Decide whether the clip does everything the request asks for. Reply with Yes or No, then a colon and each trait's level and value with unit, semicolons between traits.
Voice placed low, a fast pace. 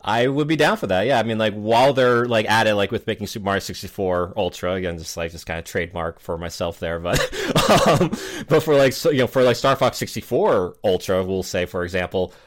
Yes: low, 110 Hz; fast, 240 wpm